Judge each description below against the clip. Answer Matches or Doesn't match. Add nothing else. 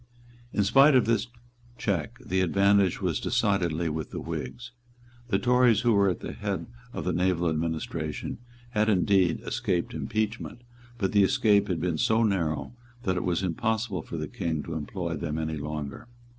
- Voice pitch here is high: Doesn't match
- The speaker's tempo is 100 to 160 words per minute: Doesn't match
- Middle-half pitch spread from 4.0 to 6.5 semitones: Matches